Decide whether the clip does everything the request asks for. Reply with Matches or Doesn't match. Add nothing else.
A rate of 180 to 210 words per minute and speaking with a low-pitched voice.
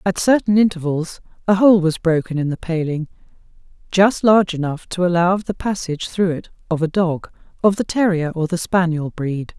Doesn't match